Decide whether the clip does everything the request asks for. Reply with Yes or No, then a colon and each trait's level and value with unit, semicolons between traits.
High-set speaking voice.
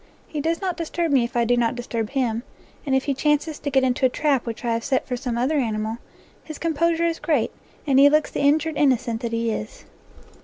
Yes: very high, 265 Hz